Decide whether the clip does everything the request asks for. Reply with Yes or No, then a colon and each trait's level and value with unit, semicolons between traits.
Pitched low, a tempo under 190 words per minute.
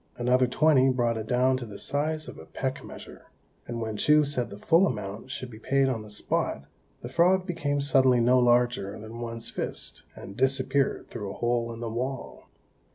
No: low, 125 Hz; average, 195 wpm